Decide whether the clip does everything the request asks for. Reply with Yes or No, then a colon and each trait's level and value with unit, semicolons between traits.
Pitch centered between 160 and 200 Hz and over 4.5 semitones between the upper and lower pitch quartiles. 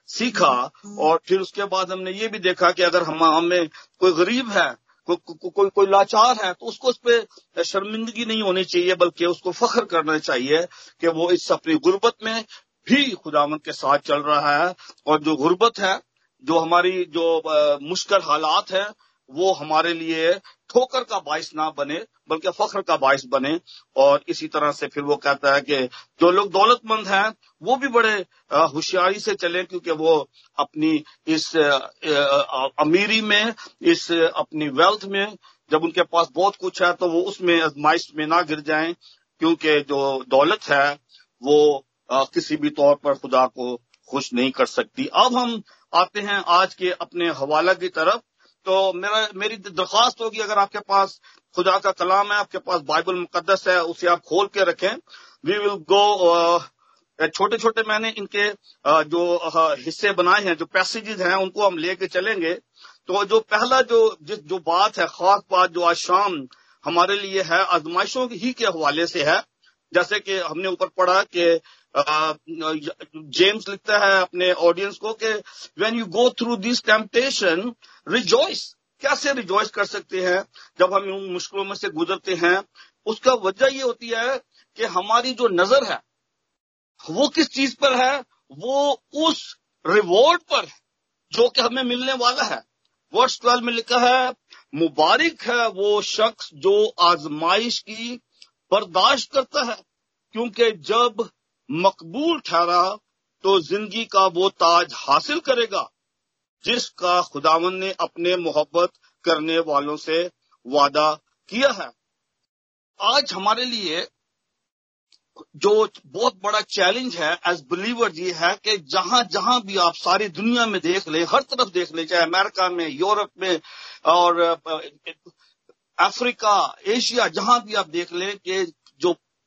Yes: high, 190 Hz; average, 5.2 semitones